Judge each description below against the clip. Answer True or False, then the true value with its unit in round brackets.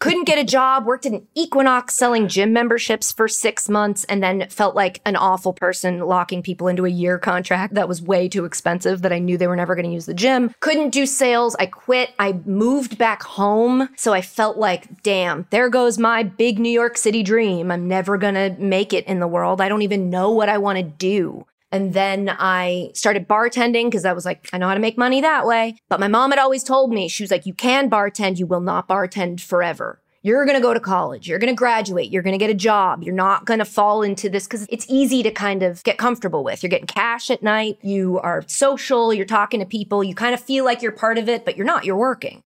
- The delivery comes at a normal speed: False (245 wpm)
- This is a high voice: True (205 Hz)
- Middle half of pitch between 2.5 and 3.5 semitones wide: False (4.1 semitones)